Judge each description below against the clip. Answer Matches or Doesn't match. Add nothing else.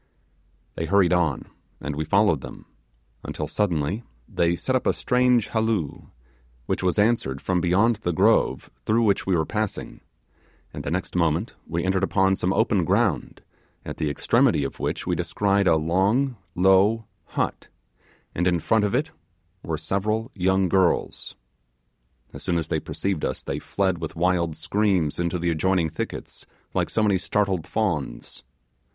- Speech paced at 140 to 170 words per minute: Matches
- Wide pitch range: Doesn't match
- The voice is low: Matches